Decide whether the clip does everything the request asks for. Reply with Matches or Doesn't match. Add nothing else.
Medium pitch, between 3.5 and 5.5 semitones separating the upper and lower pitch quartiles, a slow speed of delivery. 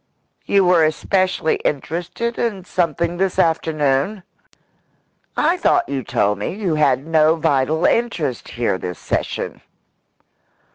Matches